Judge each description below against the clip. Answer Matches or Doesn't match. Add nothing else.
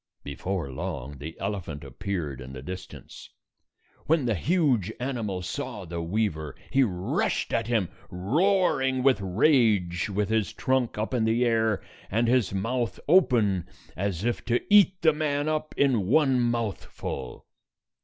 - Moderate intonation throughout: Doesn't match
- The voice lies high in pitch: Doesn't match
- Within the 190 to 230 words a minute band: Doesn't match